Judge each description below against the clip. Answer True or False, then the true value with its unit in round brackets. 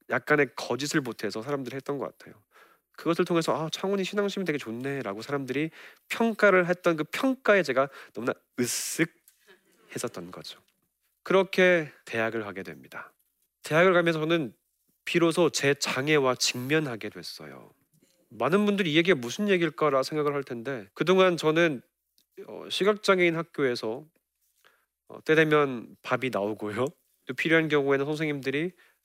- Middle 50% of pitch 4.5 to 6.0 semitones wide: True (5.1 semitones)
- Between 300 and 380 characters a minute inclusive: True (315 characters per minute)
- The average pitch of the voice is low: False (150 Hz)